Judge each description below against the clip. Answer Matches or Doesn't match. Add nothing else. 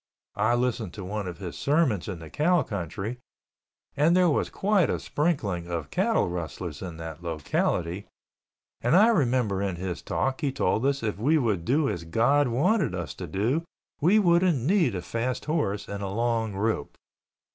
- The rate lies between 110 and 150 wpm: Doesn't match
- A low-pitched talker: Matches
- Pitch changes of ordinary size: Doesn't match